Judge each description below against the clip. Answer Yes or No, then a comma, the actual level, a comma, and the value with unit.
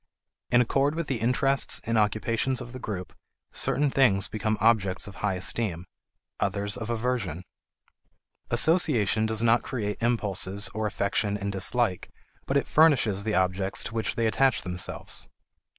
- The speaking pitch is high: No, low, 110 Hz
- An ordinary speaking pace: Yes, average, 150 wpm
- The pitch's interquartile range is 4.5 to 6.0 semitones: No, average, 3.6 semitones